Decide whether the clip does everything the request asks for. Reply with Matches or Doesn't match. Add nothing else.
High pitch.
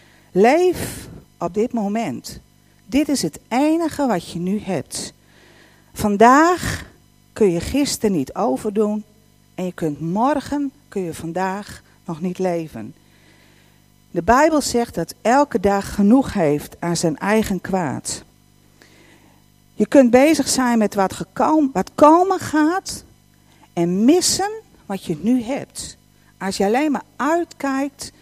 Matches